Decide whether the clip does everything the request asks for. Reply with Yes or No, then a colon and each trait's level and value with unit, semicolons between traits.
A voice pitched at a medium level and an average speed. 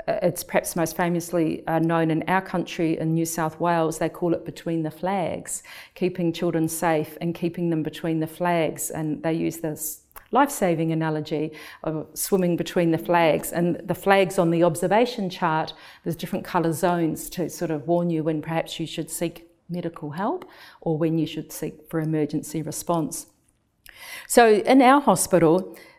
Yes: medium, 165 Hz; average, 170 wpm